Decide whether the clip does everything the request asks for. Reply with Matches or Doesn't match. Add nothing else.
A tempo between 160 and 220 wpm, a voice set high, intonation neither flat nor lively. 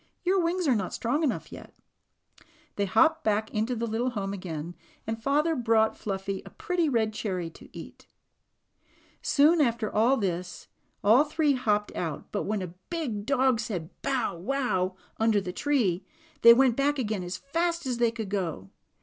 Doesn't match